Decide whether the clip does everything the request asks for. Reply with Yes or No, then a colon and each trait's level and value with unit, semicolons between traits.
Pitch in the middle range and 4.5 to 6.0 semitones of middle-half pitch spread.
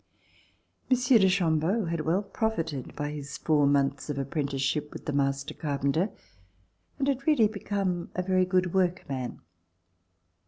Yes: medium, 165 Hz; wide, 5.4 semitones